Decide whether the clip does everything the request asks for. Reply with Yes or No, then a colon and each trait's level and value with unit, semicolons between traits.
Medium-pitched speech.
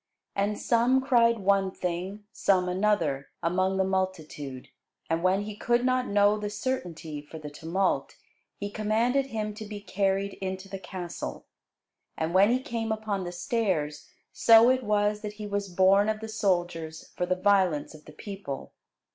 No: high, 200 Hz